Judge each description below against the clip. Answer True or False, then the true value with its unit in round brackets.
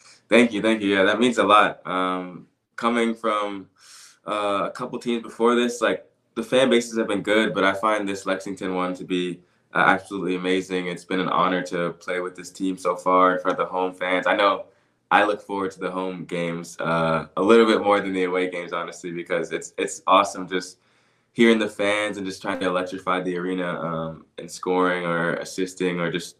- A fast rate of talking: True (215 wpm)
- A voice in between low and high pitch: False (95 Hz)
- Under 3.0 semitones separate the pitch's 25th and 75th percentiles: True (2.4 semitones)